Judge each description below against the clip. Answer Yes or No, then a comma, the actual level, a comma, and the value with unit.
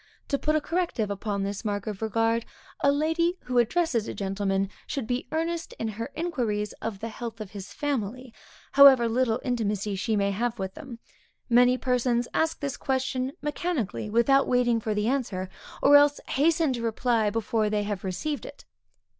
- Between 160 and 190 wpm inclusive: Yes, average, 175 wpm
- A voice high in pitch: Yes, high, 235 Hz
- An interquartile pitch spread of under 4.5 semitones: No, average, 4.8 semitones